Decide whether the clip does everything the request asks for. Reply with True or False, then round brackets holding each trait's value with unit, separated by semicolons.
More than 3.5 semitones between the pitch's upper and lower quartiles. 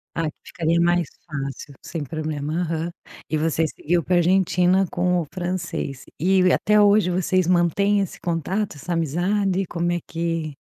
False (2.4 semitones)